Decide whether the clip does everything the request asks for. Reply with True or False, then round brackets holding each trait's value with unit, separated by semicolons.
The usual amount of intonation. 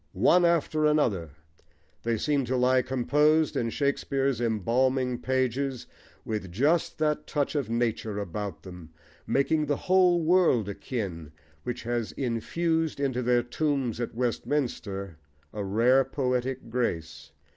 True (4.3 semitones)